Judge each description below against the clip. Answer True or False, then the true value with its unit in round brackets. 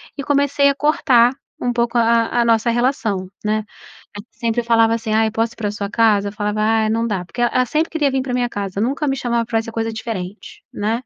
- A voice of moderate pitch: False (230 Hz)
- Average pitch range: False (2.2 semitones)